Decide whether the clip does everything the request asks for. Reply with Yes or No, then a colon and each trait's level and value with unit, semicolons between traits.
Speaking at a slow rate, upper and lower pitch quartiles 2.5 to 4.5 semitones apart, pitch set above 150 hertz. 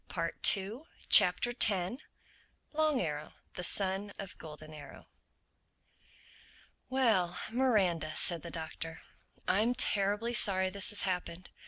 No: slow, 110 wpm; average, 4.9 semitones; high, 190 Hz